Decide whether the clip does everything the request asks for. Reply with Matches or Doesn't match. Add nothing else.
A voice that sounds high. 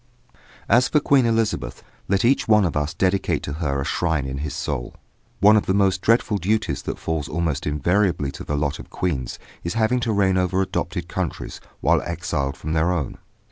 Doesn't match